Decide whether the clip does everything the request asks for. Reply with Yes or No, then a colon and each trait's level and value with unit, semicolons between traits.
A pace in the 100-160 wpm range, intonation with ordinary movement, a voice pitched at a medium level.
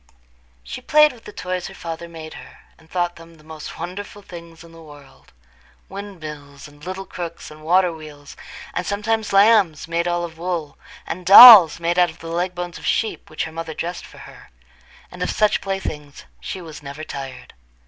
No: average, 190 wpm; average, 3.0 semitones; medium, 170 Hz